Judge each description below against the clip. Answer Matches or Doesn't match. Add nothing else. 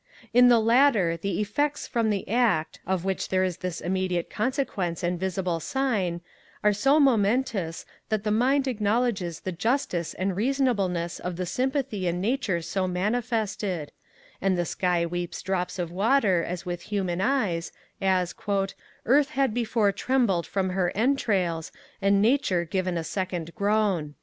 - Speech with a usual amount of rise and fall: Matches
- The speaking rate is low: Doesn't match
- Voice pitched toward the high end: Matches